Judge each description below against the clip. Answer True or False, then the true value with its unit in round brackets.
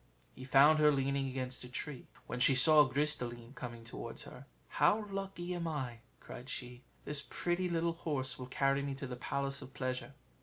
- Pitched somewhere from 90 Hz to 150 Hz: True (135 Hz)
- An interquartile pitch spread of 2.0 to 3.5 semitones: True (3.1 semitones)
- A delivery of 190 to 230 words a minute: True (195 wpm)